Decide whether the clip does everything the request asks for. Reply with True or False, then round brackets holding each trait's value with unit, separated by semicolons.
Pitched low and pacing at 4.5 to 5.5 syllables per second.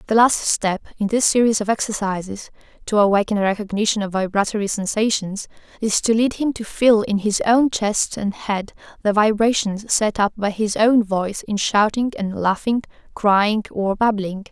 False (210 Hz; 4.9 syllables/s)